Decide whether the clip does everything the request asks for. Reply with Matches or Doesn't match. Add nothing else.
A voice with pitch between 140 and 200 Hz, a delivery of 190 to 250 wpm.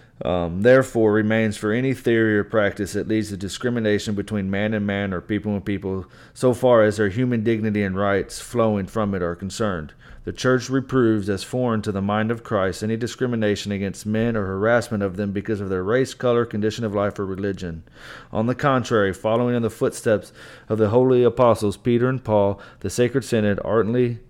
Doesn't match